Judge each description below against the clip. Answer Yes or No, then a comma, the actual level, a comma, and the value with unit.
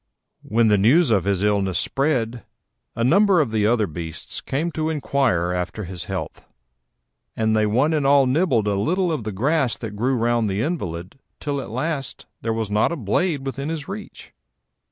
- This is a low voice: Yes, low, 120 Hz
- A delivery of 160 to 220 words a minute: Yes, average, 185 wpm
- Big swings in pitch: Yes, wide, 6.3 semitones